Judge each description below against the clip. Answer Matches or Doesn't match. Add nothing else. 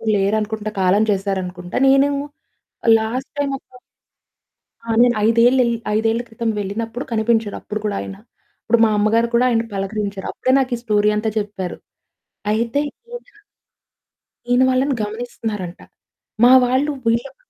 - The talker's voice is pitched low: Doesn't match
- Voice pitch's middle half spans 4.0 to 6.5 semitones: Doesn't match